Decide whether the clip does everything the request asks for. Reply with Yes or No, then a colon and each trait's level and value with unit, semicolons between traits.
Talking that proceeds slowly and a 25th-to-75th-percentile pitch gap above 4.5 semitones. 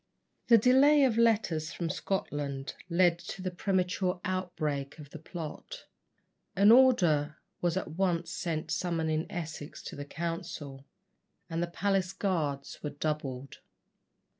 No: slow, 130 wpm; average, 3.9 semitones